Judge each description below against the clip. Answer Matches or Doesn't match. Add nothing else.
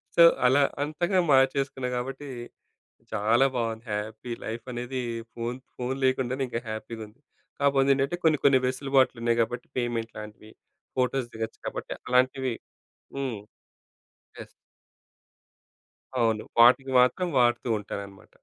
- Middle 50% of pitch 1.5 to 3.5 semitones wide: Matches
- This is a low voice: Matches